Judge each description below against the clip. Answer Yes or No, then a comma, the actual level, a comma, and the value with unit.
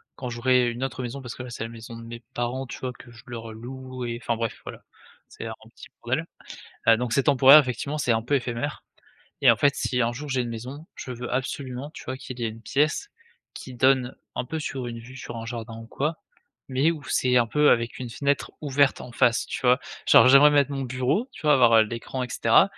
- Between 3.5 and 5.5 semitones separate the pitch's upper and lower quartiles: No, narrow, 2.5 semitones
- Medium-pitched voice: No, low, 125 Hz